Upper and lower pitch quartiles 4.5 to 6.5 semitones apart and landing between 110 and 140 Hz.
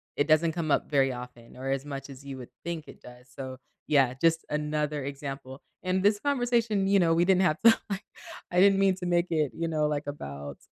No: average, 4.9 semitones; medium, 150 Hz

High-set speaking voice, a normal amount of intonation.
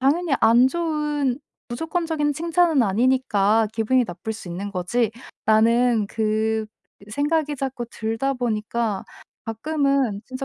Yes: high, 245 Hz; average, 4.9 semitones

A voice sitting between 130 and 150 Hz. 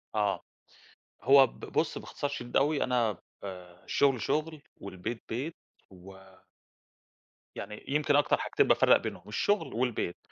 No: low, 120 Hz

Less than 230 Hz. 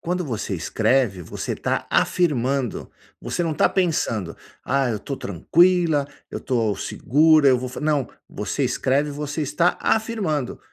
Yes: medium, 140 Hz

